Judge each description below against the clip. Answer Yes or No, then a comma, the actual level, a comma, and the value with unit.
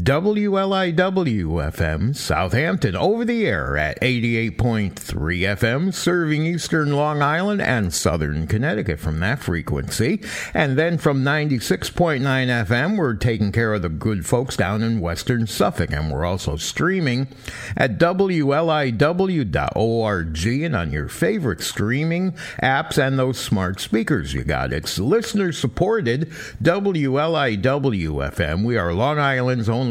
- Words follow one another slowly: Yes, slow, 125 wpm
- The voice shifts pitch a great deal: Yes, wide, 7.6 semitones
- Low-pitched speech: Yes, low, 125 Hz